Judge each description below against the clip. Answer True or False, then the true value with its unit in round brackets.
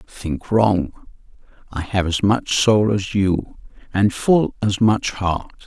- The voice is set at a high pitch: False (100 Hz)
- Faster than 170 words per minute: False (140 wpm)